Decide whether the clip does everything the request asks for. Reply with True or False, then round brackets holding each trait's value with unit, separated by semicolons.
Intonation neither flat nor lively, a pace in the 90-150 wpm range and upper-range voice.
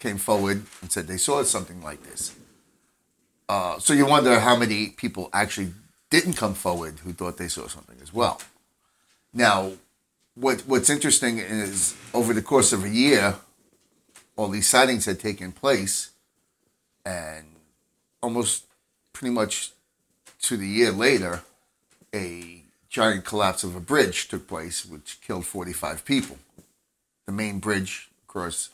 False (3.7 semitones; 145 wpm; 100 Hz)